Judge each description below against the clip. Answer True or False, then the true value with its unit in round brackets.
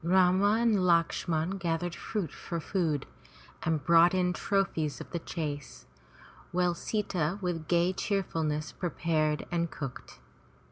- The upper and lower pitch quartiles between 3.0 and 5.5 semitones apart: False (2.6 semitones)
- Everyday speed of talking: False (125 wpm)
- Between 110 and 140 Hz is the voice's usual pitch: False (170 Hz)